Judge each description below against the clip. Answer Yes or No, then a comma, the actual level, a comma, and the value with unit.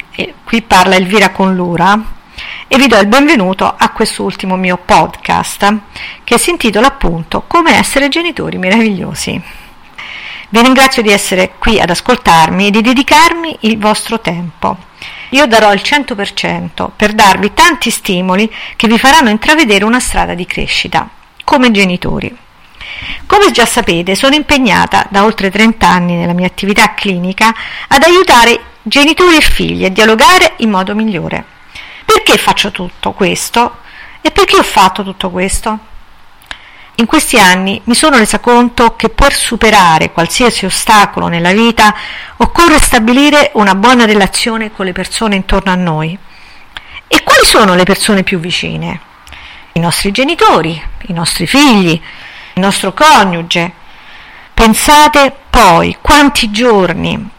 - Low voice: No, high, 215 Hz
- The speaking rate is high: No, average, 140 wpm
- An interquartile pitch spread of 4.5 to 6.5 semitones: Yes, average, 5.3 semitones